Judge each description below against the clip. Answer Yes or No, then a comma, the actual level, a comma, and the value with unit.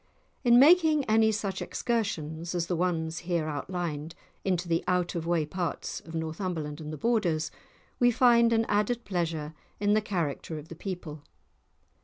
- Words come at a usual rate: Yes, average, 165 wpm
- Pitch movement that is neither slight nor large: Yes, average, 5.0 semitones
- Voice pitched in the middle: Yes, medium, 175 Hz